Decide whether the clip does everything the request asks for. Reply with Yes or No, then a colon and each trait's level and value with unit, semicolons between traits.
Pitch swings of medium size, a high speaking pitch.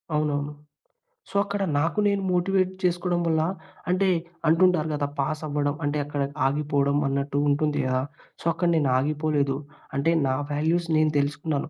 No: average, 3.3 semitones; medium, 150 Hz